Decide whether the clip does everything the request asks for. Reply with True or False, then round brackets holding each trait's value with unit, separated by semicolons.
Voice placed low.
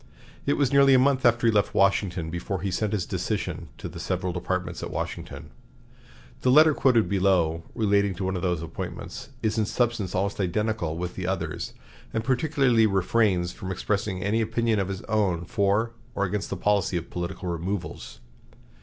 True (100 Hz)